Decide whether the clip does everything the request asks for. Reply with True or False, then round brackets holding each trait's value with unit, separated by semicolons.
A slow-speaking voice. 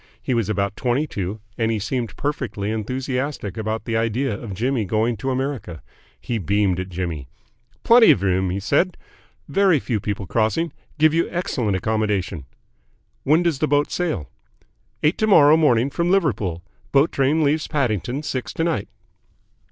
False (160 wpm)